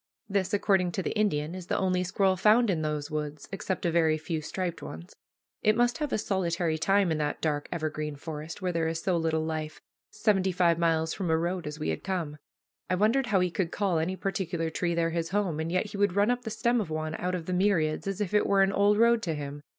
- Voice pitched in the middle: Yes, medium, 175 Hz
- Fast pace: Yes, fast, 245 wpm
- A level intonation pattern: No, average, 3.7 semitones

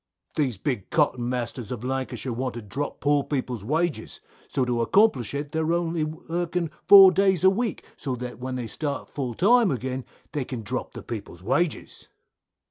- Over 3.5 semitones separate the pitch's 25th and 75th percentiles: Yes, average, 5.1 semitones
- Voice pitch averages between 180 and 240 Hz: No, low, 135 Hz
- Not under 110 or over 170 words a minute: No, average, 180 wpm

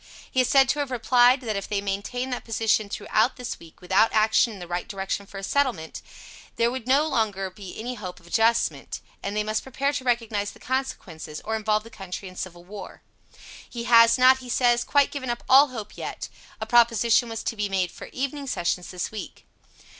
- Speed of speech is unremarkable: No, fast, 210 wpm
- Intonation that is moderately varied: Yes, average, 4.1 semitones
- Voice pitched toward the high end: Yes, high, 225 Hz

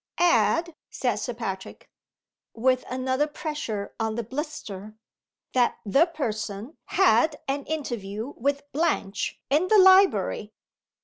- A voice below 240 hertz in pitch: No, very high, 260 Hz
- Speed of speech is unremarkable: No, slow, 115 wpm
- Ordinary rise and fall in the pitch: No, wide, 6.2 semitones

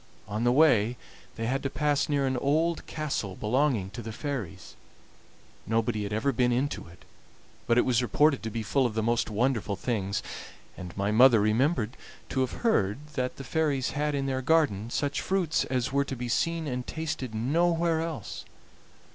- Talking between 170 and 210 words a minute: Yes, average, 180 wpm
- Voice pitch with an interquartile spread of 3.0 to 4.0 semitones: No, average, 4.8 semitones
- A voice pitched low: Yes, low, 130 Hz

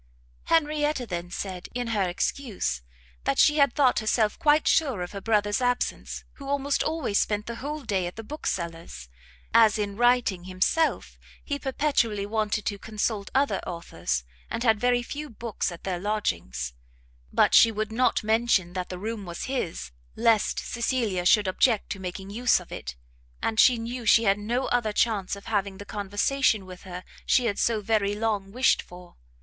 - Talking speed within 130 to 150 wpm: No, average, 175 wpm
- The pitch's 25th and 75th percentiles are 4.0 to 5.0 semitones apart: Yes, average, 4.3 semitones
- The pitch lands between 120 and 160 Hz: No, high, 215 Hz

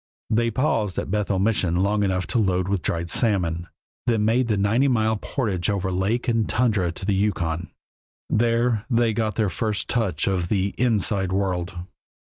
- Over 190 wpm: No, average, 170 wpm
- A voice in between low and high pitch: No, low, 100 Hz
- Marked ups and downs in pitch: No, average, 3.4 semitones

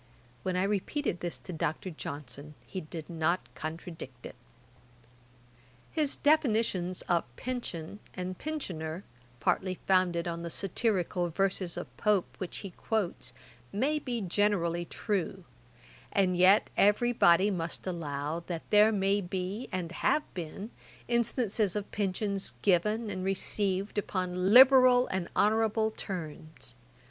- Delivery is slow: Yes, slow, 125 wpm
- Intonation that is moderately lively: Yes, average, 3.7 semitones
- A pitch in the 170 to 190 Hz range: Yes, medium, 185 Hz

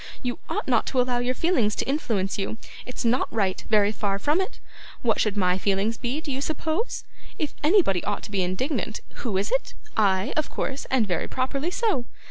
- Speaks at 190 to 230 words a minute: Yes, average, 200 wpm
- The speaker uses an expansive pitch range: Yes, wide, 5.9 semitones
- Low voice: No, high, 240 Hz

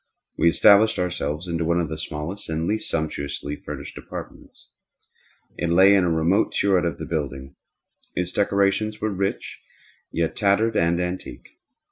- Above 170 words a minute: No, average, 150 wpm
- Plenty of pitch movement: No, average, 3.7 semitones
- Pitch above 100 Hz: No, very low, 85 Hz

